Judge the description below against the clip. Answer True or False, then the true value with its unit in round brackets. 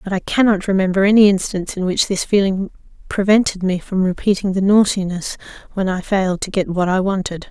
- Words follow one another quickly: False (190 wpm)